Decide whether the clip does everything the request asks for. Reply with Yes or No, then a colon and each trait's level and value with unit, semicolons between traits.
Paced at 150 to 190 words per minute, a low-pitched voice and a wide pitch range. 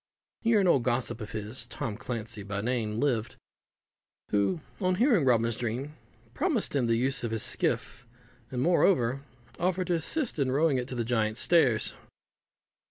Yes: average, 165 wpm; low, 125 Hz; wide, 6.3 semitones